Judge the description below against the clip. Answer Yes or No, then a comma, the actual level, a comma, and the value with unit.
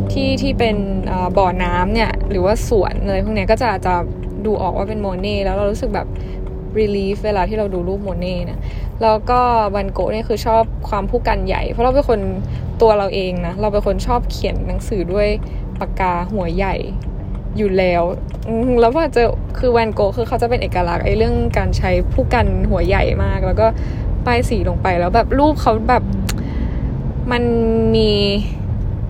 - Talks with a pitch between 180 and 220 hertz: Yes, high, 190 Hz